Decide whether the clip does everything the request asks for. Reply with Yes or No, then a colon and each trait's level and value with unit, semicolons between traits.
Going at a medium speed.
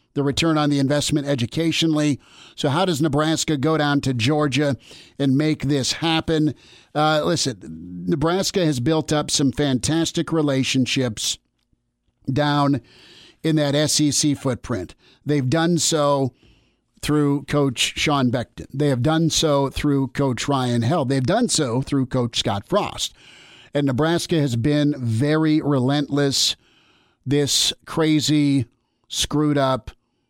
No: slow, 125 wpm